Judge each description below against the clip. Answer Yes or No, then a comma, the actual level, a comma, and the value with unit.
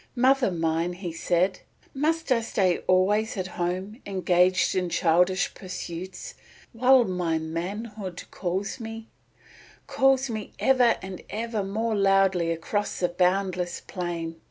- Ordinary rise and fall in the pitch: Yes, average, 4.0 semitones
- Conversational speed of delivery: No, slow, 125 wpm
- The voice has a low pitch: No, high, 190 Hz